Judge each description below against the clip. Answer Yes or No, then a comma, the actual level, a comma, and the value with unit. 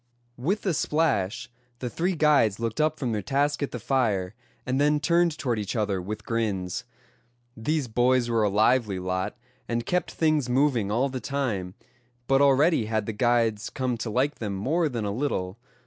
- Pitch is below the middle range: Yes, low, 120 Hz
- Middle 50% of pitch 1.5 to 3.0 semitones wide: No, average, 5.2 semitones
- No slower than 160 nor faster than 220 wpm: Yes, average, 180 wpm